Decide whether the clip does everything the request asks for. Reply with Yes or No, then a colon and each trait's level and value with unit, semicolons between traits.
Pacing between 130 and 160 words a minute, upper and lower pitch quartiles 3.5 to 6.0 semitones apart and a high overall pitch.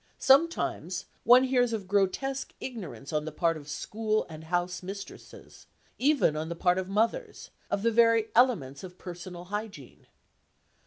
Yes: average, 150 wpm; average, 5.1 semitones; high, 195 Hz